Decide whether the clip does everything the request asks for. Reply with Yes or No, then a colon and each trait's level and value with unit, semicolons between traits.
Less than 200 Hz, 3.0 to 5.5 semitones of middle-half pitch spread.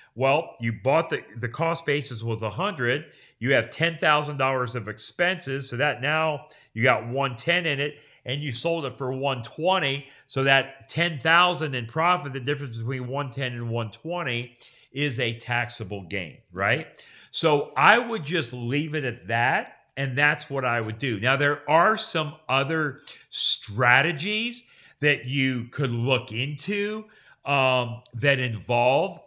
Yes: low, 135 Hz; average, 4.1 semitones